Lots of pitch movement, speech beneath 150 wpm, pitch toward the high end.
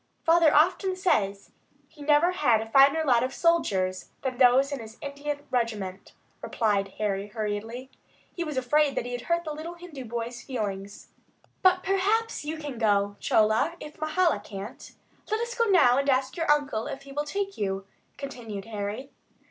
No: wide, 6.5 semitones; average, 170 wpm; very high, 270 Hz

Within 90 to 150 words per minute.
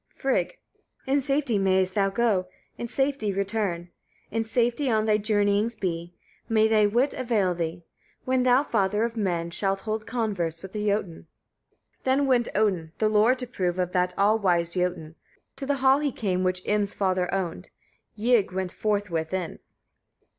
No: average, 170 wpm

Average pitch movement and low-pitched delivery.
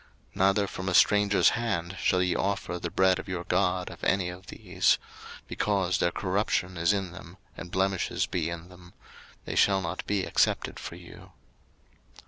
No: narrow, 1.7 semitones; very low, 95 Hz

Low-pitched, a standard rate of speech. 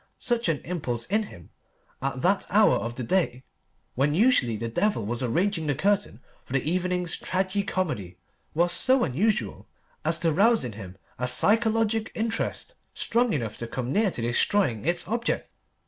No: medium, 175 Hz; average, 165 wpm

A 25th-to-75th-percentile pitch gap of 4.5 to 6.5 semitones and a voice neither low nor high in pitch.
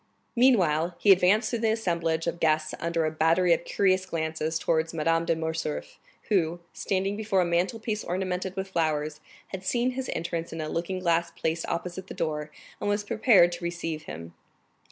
No: average, 3.0 semitones; medium, 170 Hz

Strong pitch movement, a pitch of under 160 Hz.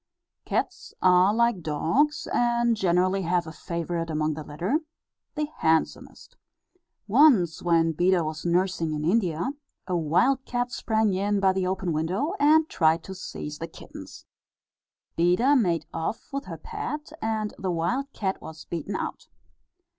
No: wide, 6.1 semitones; medium, 185 Hz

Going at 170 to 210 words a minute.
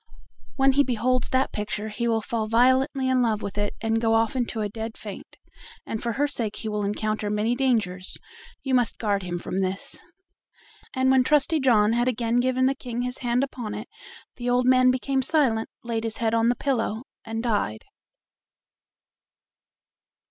Yes: average, 180 wpm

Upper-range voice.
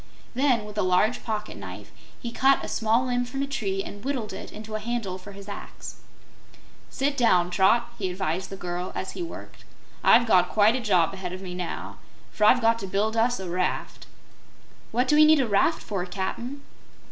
Yes: high, 215 Hz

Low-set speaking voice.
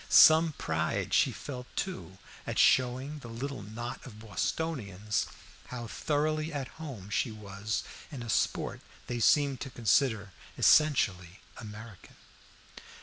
Yes: low, 120 Hz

